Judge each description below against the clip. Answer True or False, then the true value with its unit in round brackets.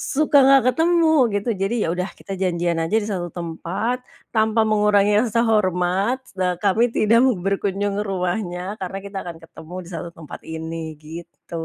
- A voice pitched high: True (195 Hz)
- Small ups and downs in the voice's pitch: False (3.8 semitones)